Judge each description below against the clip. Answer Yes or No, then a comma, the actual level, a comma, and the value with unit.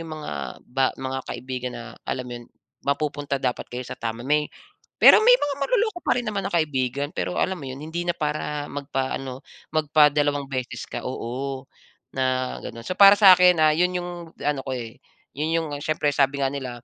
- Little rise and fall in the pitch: No, average, 3.7 semitones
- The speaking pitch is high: No, medium, 145 Hz